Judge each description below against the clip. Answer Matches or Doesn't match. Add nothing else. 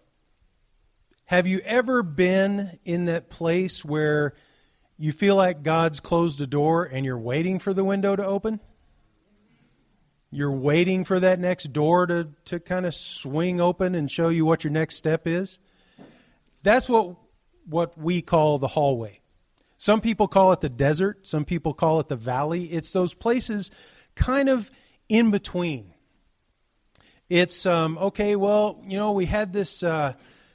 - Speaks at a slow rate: Doesn't match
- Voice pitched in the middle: Matches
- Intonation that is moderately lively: Matches